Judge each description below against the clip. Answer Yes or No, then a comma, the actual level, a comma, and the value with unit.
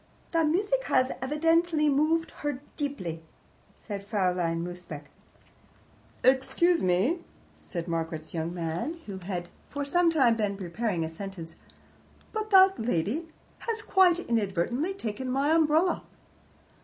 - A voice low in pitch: No, very high, 250 Hz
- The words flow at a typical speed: No, slow, 120 wpm